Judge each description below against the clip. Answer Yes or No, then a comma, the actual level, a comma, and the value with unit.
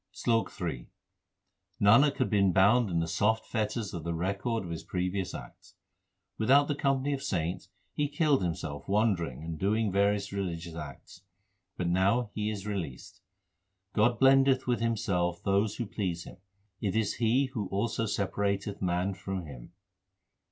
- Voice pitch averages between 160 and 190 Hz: No, low, 100 Hz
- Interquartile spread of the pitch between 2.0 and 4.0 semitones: No, average, 4.4 semitones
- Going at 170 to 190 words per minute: No, average, 160 wpm